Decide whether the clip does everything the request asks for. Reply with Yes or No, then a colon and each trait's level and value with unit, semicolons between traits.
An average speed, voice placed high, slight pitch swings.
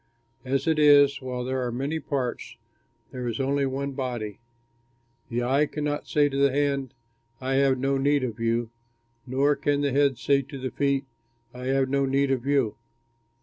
No: average, 180 wpm; low, 135 Hz; narrow, 1.8 semitones